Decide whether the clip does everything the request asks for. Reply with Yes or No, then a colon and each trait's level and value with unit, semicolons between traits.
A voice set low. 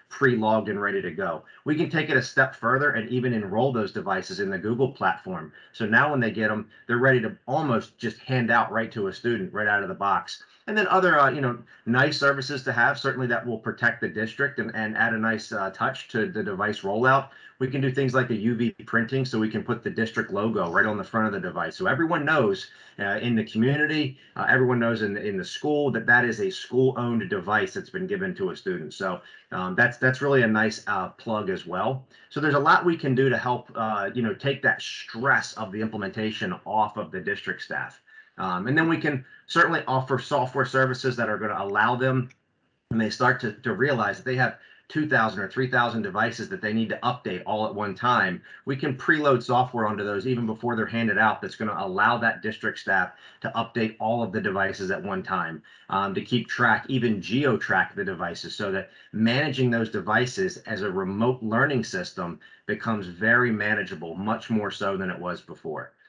Yes: low, 125 Hz